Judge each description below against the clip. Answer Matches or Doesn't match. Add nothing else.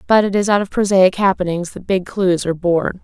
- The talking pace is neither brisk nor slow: Doesn't match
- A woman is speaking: Matches